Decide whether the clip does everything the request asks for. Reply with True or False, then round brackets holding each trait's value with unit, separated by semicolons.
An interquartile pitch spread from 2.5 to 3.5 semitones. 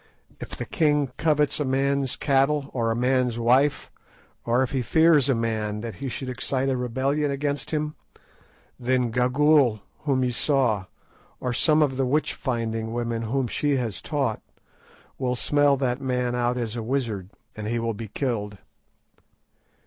True (3.1 semitones)